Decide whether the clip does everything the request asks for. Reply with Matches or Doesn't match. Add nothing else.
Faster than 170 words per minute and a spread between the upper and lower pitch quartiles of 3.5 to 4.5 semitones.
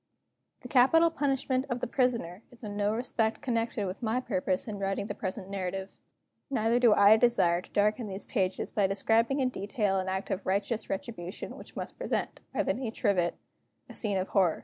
Matches